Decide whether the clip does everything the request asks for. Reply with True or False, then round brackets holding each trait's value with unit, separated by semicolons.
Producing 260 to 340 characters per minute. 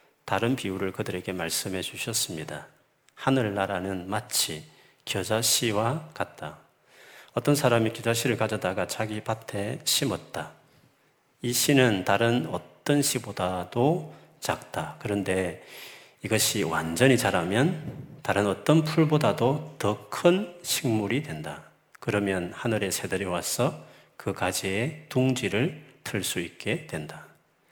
False (245 characters per minute)